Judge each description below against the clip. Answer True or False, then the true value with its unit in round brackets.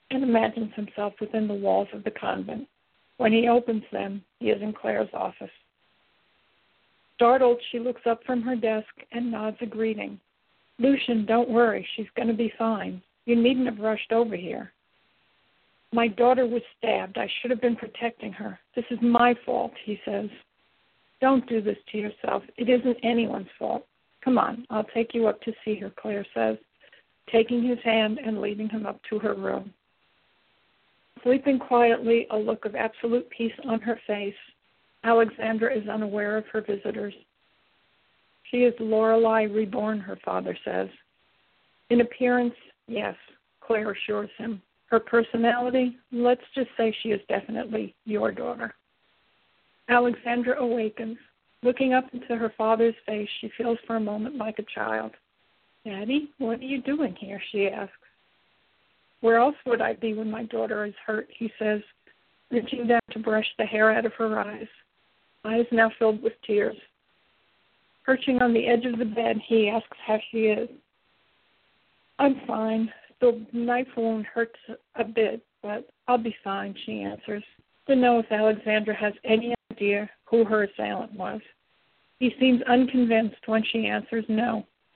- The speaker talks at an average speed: True (155 wpm)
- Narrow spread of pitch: True (1.9 semitones)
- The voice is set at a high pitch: True (225 Hz)